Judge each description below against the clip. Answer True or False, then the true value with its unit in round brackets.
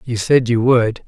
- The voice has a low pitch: True (120 Hz)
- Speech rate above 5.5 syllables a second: False (4.1 syllables/s)